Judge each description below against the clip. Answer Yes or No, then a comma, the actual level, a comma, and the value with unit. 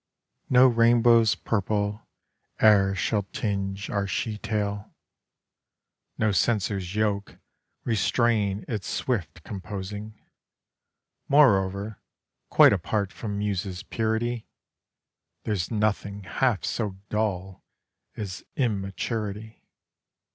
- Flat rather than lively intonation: Yes, narrow, 2.1 semitones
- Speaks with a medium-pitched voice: No, low, 105 Hz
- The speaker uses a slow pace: Yes, slow, 85 wpm